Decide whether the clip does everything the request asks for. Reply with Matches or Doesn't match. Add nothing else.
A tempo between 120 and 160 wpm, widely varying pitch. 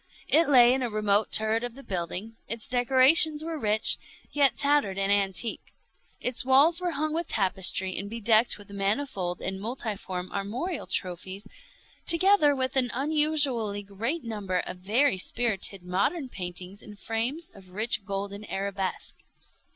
Matches